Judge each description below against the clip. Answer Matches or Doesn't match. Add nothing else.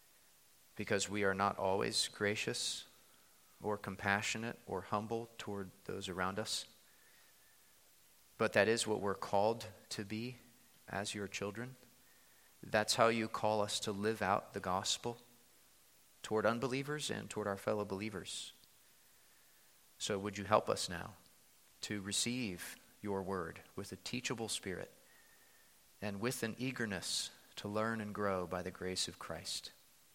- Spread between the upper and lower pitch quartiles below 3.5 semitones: Matches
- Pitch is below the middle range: Matches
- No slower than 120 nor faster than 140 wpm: Matches